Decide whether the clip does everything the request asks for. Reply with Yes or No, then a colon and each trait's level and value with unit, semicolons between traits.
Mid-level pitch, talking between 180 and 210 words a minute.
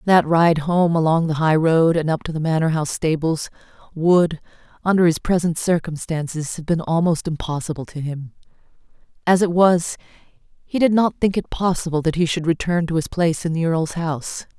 Yes: medium, 165 Hz; average, 185 wpm